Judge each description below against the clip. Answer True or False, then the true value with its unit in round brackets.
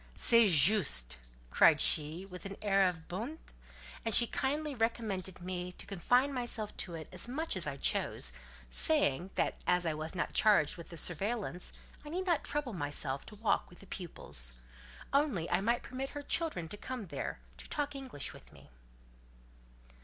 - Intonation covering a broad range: True (6.7 semitones)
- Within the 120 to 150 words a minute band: False (175 wpm)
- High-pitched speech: True (195 Hz)